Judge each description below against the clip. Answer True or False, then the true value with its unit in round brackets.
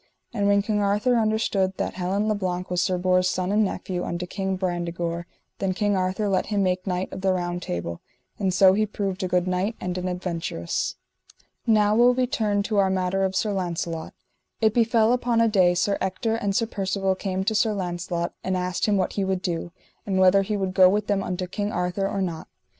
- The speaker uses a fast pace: True (215 wpm)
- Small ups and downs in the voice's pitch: True (2.3 semitones)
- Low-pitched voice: False (190 Hz)